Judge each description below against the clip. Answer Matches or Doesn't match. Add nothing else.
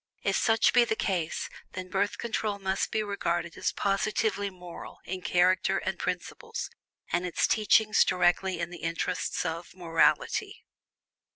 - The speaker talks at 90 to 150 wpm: Matches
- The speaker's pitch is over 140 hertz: Matches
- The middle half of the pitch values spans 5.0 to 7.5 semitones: Doesn't match